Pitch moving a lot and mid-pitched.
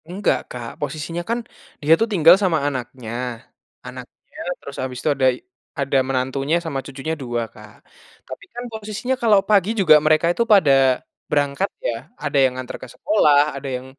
Yes: wide, 5.8 semitones; medium, 145 Hz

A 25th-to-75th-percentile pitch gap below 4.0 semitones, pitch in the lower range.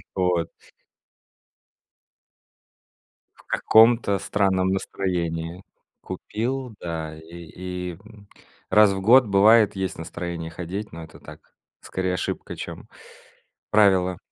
Yes: average, 3.5 semitones; very low, 95 Hz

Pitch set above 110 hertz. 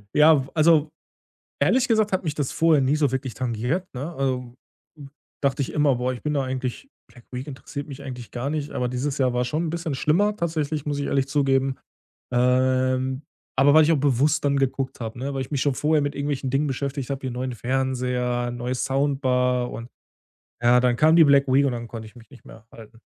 Yes: low, 135 Hz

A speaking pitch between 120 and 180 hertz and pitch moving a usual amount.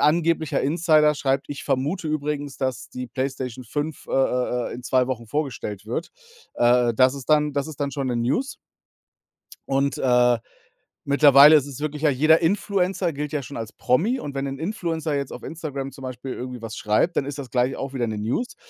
Yes: medium, 140 Hz; average, 3.3 semitones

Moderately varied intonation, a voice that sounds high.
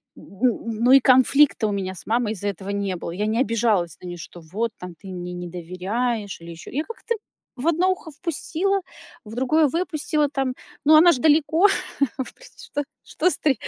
No: wide, 8.0 semitones; high, 235 Hz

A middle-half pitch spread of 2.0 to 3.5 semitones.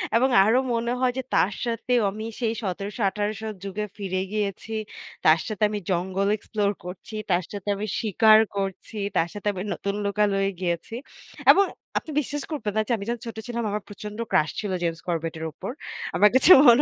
Yes: average, 2.9 semitones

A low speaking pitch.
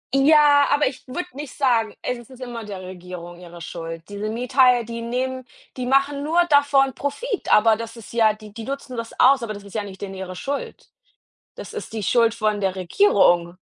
No: high, 230 Hz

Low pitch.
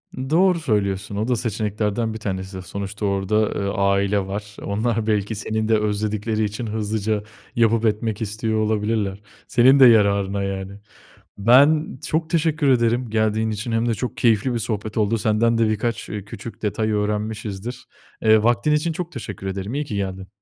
Yes: low, 110 Hz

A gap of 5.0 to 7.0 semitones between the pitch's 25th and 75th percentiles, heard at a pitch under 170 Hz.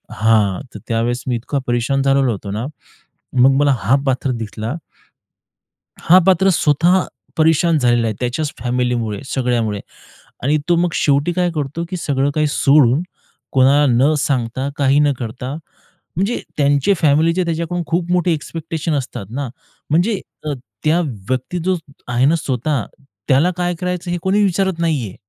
Yes: average, 5.3 semitones; medium, 140 Hz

